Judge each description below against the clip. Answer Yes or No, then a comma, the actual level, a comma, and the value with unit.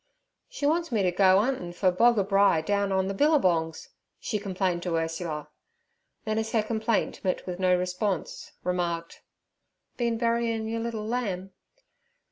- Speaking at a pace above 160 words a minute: No, average, 145 wpm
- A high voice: Yes, high, 195 Hz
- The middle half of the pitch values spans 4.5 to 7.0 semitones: No, average, 3.9 semitones